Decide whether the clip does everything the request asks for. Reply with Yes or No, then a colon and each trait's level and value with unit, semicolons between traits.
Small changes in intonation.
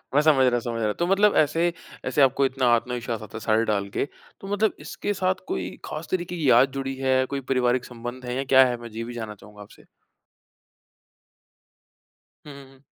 No: average, 3.9 semitones